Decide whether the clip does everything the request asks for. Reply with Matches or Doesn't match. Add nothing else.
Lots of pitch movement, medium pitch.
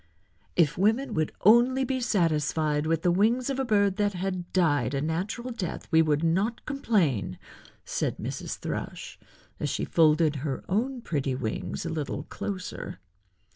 Matches